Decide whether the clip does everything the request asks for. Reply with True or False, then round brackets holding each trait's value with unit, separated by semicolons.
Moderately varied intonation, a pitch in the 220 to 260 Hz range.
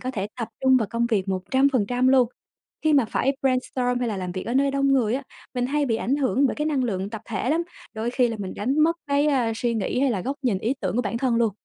True (3.5 semitones; 245 Hz)